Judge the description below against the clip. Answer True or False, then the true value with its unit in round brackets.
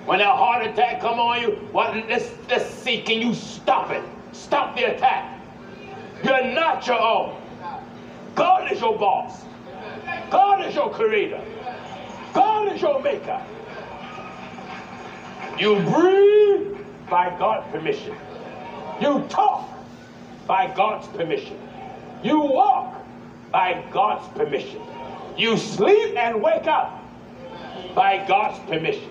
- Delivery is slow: True (115 wpm)